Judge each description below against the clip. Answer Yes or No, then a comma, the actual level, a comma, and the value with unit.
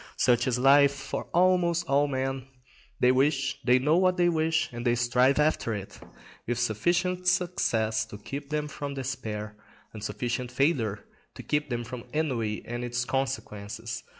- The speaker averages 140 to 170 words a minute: Yes, average, 160 wpm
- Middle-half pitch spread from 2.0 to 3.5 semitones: No, average, 4.0 semitones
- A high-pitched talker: No, low, 130 Hz